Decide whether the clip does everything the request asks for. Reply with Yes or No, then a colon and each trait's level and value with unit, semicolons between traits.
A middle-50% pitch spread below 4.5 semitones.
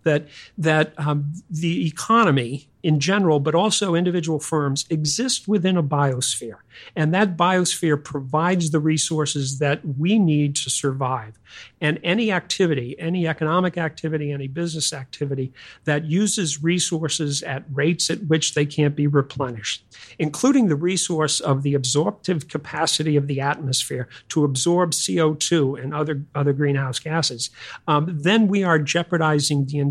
Yes: average, 3.0 semitones